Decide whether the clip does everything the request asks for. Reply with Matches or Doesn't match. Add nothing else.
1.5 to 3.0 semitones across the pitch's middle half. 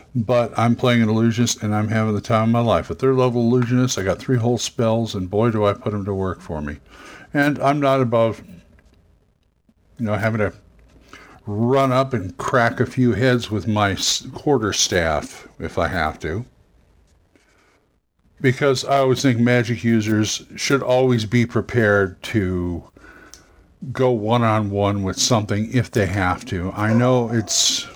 Doesn't match